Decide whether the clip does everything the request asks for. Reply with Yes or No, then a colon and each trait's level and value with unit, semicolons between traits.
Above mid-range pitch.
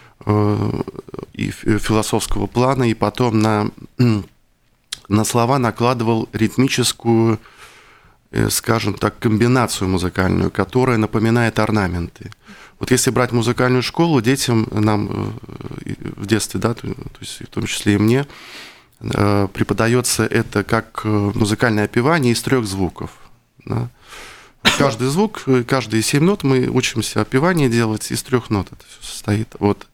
No: low, 115 Hz